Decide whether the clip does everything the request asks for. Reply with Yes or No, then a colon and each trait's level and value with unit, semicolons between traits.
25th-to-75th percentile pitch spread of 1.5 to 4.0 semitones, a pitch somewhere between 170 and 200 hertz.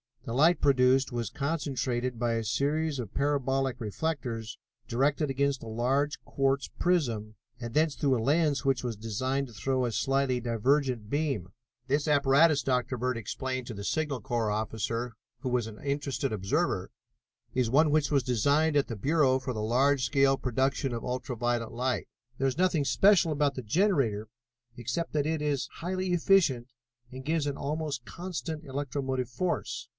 No: average, 3.4 semitones; low, 135 Hz